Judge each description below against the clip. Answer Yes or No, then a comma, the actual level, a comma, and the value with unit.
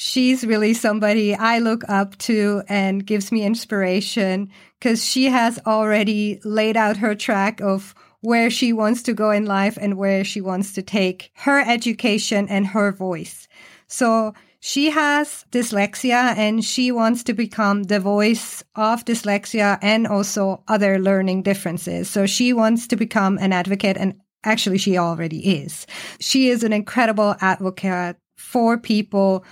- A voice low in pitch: No, high, 210 Hz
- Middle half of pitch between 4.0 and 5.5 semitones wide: No, narrow, 2.6 semitones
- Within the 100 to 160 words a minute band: Yes, average, 150 wpm